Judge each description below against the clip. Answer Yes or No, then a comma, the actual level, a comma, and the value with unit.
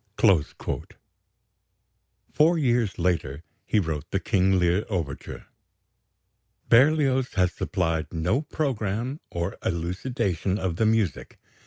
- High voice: No, very low, 95 Hz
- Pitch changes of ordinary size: No, wide, 6.3 semitones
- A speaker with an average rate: No, slow, 100 wpm